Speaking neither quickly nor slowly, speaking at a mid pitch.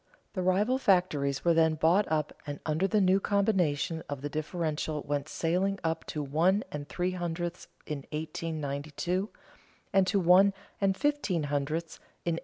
Yes: average, 155 wpm; medium, 170 Hz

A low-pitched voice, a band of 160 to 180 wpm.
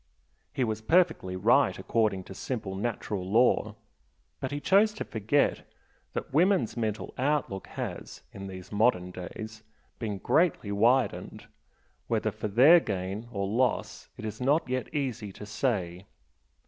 No: low, 110 Hz; average, 140 wpm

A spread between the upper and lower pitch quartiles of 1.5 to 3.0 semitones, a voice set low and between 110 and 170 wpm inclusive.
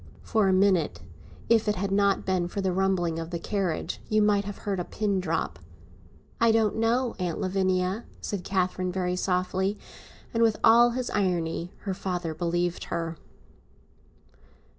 No: narrow, 2.6 semitones; high, 190 Hz; average, 160 wpm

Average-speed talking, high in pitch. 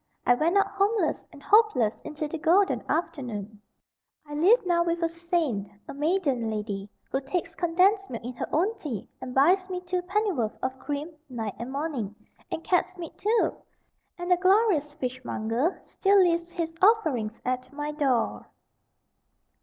Yes: average, 160 wpm; very high, 320 Hz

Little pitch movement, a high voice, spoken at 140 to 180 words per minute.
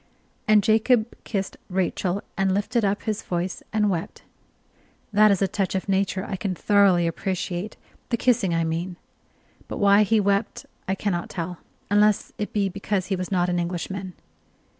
Yes: narrow, 2.3 semitones; high, 195 Hz; average, 165 wpm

